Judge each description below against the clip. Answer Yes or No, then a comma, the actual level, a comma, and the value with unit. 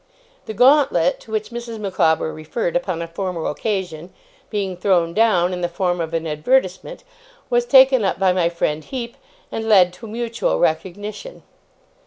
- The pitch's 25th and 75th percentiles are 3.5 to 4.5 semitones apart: No, average, 4.9 semitones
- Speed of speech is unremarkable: Yes, average, 165 wpm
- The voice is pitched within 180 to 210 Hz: Yes, high, 190 Hz